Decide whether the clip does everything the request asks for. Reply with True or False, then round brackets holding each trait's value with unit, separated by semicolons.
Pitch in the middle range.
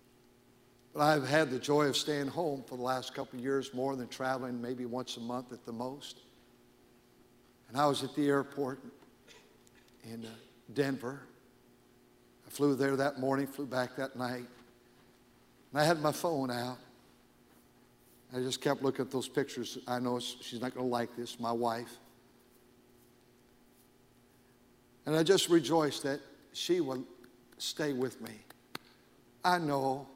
False (130 Hz)